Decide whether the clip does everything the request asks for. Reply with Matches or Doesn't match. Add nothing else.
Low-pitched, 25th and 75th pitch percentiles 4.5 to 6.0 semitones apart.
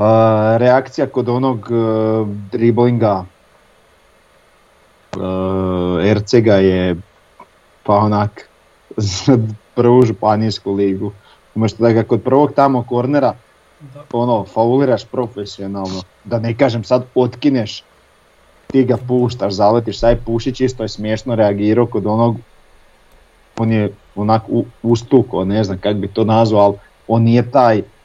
Doesn't match